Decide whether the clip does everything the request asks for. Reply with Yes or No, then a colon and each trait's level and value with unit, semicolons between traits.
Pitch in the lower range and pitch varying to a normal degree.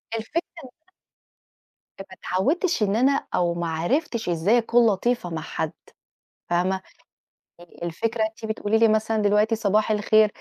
No: high, 215 Hz; average, 3.7 semitones